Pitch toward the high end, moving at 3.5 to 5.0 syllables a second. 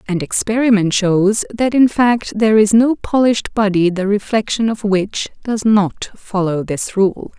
Yes: high, 210 Hz; 4.3 syllables/s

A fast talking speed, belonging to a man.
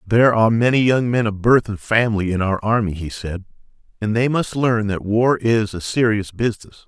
Yes: fast, 210 wpm; male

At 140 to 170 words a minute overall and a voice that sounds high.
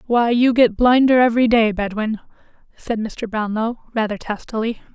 Yes: average, 145 wpm; high, 225 Hz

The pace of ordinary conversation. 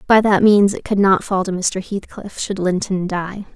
No: fast, 220 wpm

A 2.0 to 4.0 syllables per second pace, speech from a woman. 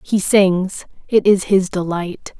Yes: 3.4 syllables/s; female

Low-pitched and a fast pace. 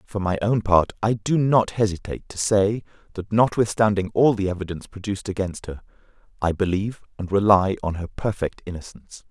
No: low, 100 Hz; average, 170 wpm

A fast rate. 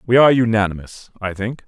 No: average, 180 wpm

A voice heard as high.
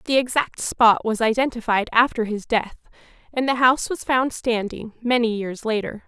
Yes: high, 230 Hz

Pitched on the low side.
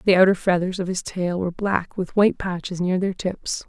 No: medium, 185 Hz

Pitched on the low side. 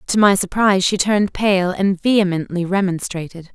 No: high, 190 Hz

